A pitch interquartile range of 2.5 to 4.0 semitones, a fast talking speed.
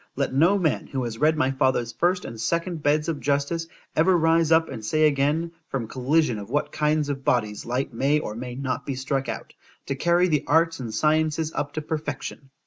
Yes: average, 3.5 semitones; fast, 210 wpm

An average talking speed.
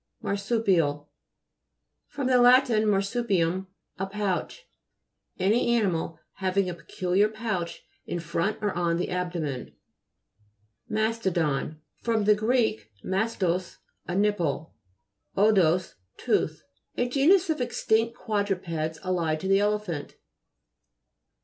No: slow, 105 wpm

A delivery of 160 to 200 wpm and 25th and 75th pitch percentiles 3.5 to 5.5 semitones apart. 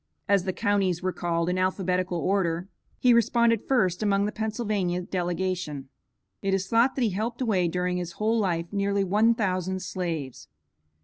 No: average, 165 wpm; average, 3.1 semitones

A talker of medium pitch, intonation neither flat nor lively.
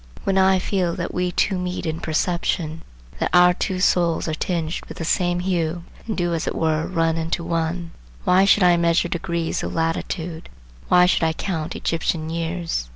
No: medium, 170 Hz; narrow, 1.7 semitones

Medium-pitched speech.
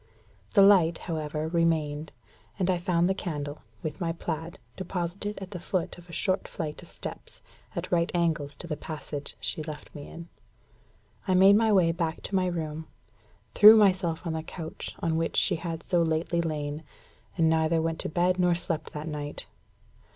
Yes: medium, 165 Hz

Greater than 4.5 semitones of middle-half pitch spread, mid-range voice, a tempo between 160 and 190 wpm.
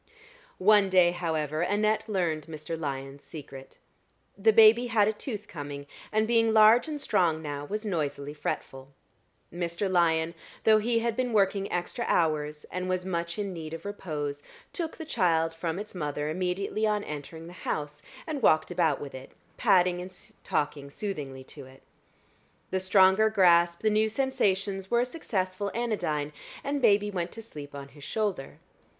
Yes: wide, 5.6 semitones; medium, 180 Hz; average, 165 wpm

